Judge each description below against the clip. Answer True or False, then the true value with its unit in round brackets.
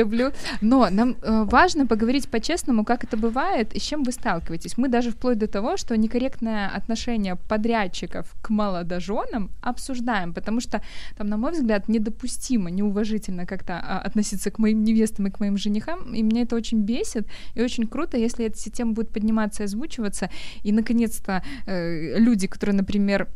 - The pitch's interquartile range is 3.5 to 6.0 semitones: False (2.6 semitones)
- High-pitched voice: True (220 Hz)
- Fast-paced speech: True (170 wpm)